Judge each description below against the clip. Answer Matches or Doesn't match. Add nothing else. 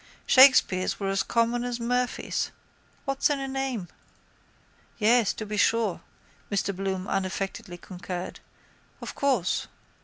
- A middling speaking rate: Doesn't match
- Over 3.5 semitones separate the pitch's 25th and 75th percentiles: Matches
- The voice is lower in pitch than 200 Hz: Doesn't match